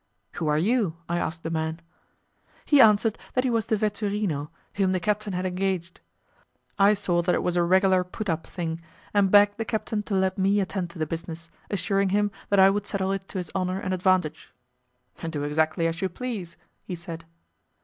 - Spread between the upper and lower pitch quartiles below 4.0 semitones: Yes, average, 3.3 semitones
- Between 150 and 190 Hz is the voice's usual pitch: Yes, medium, 185 Hz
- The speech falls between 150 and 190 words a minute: No, average, 200 wpm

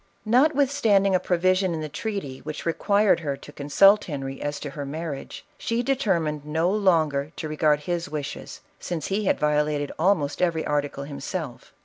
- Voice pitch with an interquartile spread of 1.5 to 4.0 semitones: No, average, 4.9 semitones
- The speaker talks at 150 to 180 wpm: Yes, average, 165 wpm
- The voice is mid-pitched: Yes, medium, 160 Hz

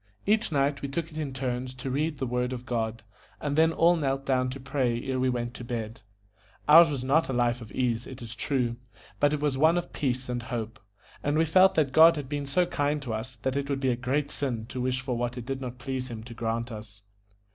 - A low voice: Yes, low, 130 Hz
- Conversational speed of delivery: No, fast, 250 wpm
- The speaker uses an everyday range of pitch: Yes, average, 3.1 semitones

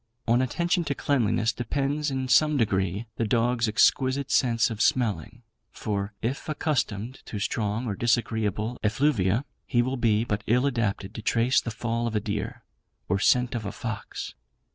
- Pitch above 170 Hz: No, low, 115 Hz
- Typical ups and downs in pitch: Yes, average, 3.4 semitones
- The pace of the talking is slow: No, average, 165 wpm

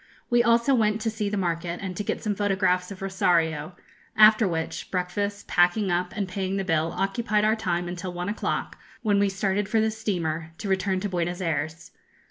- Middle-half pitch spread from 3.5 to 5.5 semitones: No, average, 3.0 semitones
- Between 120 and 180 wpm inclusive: No, average, 195 wpm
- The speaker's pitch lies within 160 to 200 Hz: Yes, high, 190 Hz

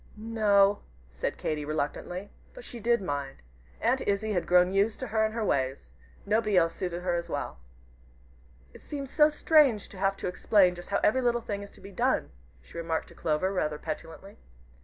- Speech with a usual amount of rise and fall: Yes, average, 4.3 semitones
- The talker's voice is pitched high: Yes, high, 195 Hz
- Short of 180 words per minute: No, average, 195 wpm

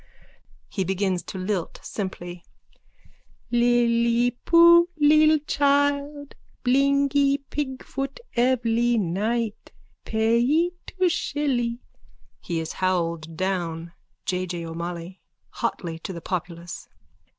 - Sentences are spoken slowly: Yes, slow, 95 wpm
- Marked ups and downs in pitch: Yes, wide, 7.6 semitones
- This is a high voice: Yes, high, 235 Hz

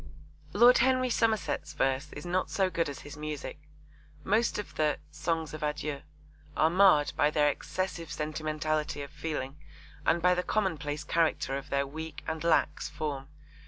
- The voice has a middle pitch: Yes, medium, 155 Hz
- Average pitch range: Yes, average, 3.3 semitones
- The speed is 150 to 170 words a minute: Yes, average, 160 wpm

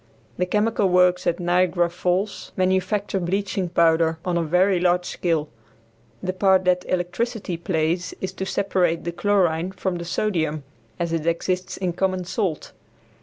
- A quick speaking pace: No, average, 150 wpm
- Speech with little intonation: Yes, narrow, 1.8 semitones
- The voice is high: No, medium, 180 Hz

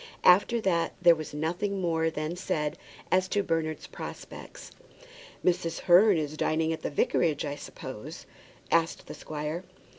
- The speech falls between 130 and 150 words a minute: Yes, average, 145 wpm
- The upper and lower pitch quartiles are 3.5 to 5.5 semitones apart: No, narrow, 2.5 semitones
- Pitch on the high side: No, medium, 165 Hz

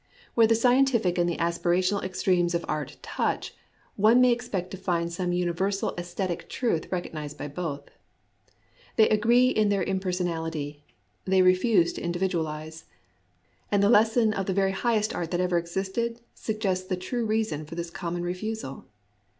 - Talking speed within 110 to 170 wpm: Yes, average, 160 wpm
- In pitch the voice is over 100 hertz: Yes, medium, 185 Hz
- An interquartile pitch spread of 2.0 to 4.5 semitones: Yes, average, 4.0 semitones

